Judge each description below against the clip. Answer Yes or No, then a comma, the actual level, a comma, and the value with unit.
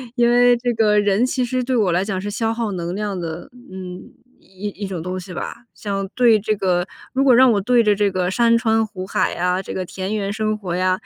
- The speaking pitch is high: Yes, high, 205 Hz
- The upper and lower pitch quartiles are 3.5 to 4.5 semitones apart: Yes, average, 3.8 semitones